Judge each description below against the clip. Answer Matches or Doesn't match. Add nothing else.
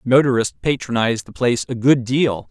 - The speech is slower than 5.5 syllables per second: Doesn't match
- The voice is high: Doesn't match